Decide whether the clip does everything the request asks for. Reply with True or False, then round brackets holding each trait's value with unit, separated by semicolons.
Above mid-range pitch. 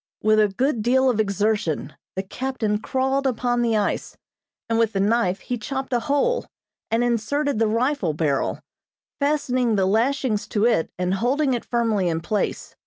True (230 Hz)